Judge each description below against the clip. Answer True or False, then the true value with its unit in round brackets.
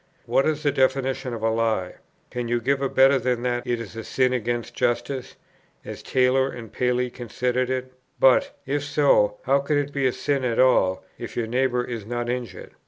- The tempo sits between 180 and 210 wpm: True (200 wpm)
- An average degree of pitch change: False (1.9 semitones)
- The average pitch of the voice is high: False (125 Hz)